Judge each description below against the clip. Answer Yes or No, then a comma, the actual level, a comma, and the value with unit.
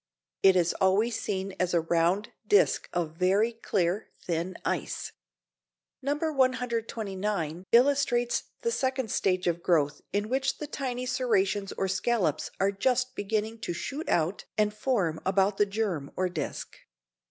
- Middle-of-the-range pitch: No, high, 205 Hz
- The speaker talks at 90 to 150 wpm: Yes, average, 140 wpm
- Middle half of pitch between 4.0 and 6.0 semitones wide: Yes, average, 4.9 semitones